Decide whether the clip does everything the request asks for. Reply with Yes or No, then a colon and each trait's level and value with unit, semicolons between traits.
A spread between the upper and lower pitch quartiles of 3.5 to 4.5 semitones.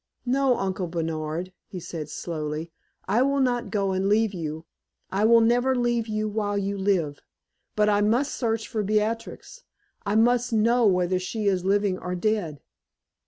Yes: average, 4.0 semitones